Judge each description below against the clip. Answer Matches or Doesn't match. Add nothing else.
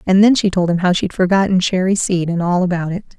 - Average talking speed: Doesn't match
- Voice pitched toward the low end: Doesn't match